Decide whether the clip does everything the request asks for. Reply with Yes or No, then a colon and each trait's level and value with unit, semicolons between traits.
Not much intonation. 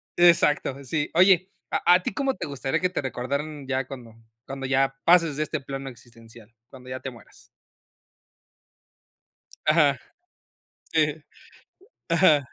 No: average, 4.0 semitones